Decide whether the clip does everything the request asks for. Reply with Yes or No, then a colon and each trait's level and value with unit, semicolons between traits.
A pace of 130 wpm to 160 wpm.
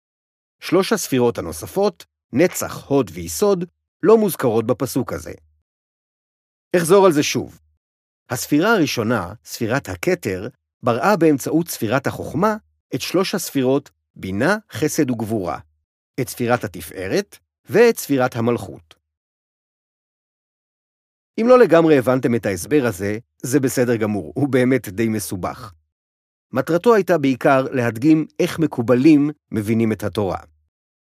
No: average, 110 wpm